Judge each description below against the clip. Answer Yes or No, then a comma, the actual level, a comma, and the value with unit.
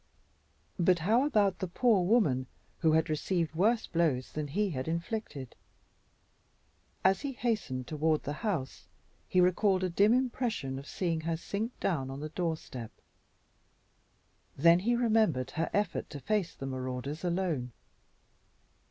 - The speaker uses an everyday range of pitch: No, wide, 6.1 semitones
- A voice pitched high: No, medium, 170 Hz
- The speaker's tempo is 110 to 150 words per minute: Yes, average, 140 wpm